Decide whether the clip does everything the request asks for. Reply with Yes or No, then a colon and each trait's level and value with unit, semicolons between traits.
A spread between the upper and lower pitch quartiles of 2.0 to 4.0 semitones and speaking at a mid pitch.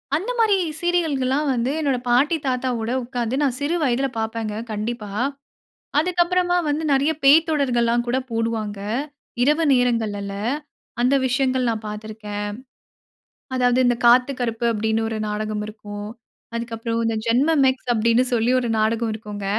No: average, 3.6 semitones; high, 240 Hz